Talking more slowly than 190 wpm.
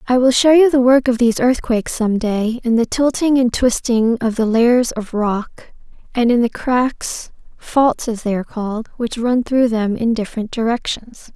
No: average, 195 wpm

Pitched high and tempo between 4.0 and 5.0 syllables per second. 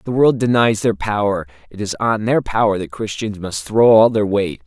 No: low, 105 Hz; 4.8 syllables/s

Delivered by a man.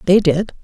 No: female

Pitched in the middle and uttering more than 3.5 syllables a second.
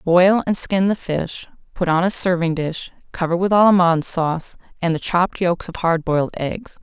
Yes: medium, 175 Hz; 5.1 syllables/s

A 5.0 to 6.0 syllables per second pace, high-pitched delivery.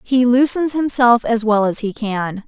No: 4.2 syllables/s; high, 235 Hz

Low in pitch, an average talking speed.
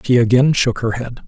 No: low, 120 Hz; fast, 235 wpm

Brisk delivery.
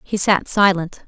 No: average, 165 wpm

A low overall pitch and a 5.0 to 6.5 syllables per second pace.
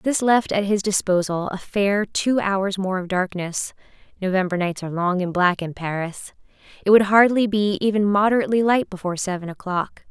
No: high, 195 Hz; 5.2 syllables/s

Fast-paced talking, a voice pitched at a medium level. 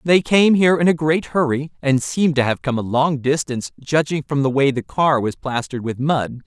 Yes: fast, 230 wpm; medium, 145 Hz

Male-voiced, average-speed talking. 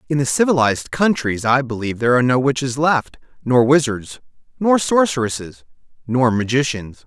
Yes: male; average, 145 wpm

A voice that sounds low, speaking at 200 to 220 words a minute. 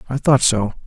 Yes: low, 125 Hz; fast, 210 wpm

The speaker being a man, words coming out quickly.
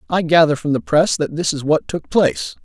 Yes: male; fast, 250 wpm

